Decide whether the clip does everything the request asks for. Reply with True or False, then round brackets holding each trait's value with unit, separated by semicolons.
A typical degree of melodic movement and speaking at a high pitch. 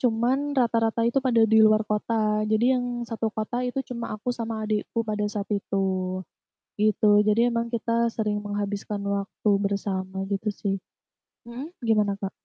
False (2.3 semitones; 220 Hz)